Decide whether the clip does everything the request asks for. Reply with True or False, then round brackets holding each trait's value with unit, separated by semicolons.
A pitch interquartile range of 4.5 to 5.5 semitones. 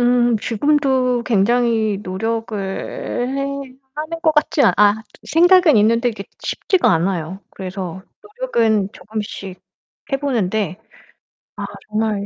True (5.2 semitones)